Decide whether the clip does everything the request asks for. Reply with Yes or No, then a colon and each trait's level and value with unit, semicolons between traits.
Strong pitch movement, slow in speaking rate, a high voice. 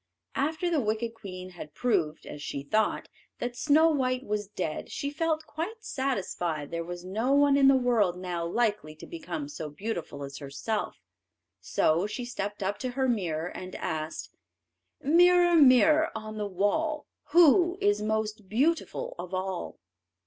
No: wide, 8.1 semitones; average, 155 wpm; high, 220 Hz